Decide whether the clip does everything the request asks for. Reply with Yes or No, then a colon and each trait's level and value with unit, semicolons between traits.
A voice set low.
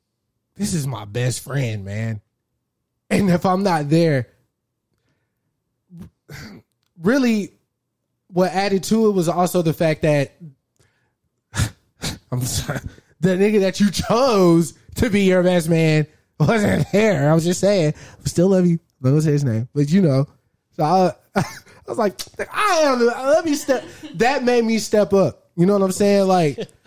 No: medium, 170 Hz